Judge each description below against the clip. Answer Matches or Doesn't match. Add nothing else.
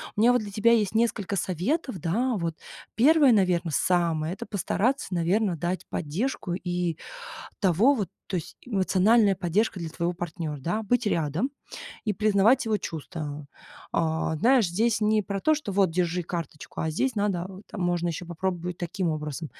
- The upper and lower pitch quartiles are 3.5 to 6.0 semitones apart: Matches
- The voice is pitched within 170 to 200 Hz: Matches